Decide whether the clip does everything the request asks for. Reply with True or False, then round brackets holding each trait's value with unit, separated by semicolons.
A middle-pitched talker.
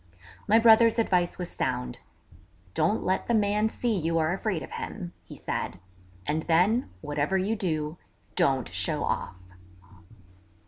True (180 Hz)